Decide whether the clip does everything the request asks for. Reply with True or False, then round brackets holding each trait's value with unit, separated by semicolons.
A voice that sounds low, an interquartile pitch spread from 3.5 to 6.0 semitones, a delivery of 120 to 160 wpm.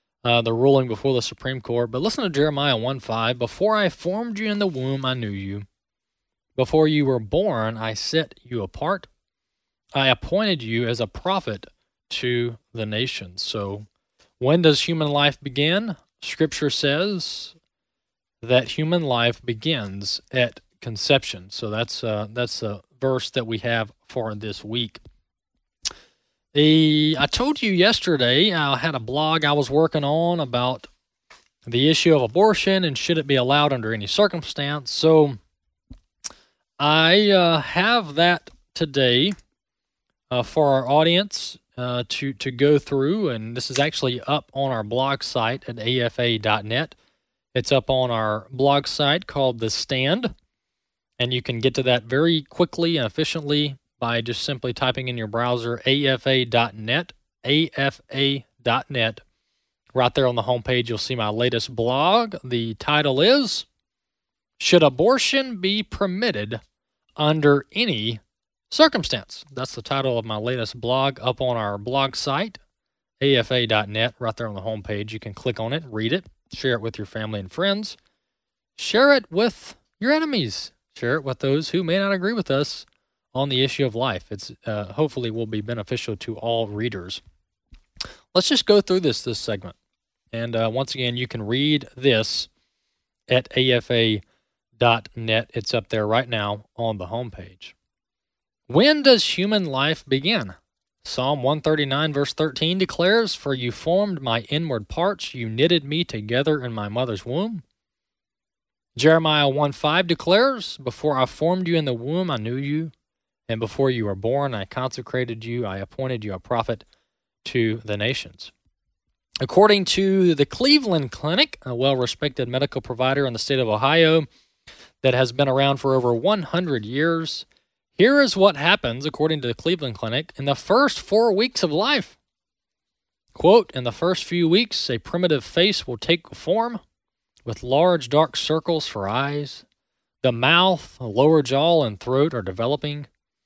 True (130 Hz; 5.3 semitones; 155 wpm)